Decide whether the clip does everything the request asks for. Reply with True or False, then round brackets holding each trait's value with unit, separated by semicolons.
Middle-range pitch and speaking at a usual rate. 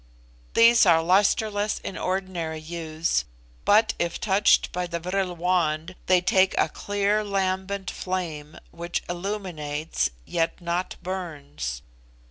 False (180 Hz; 115 wpm)